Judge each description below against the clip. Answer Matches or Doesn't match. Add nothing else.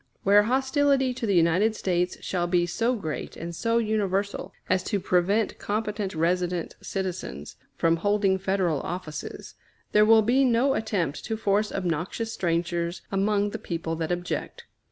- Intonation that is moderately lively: Matches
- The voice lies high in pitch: Matches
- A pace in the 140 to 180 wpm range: Matches